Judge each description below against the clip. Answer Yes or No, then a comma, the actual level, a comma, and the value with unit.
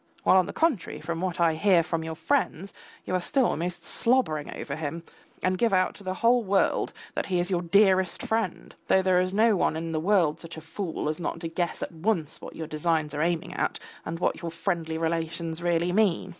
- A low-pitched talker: No, medium, 175 Hz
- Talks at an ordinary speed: No, fast, 225 wpm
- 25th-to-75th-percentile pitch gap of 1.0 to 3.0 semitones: Yes, average, 2.7 semitones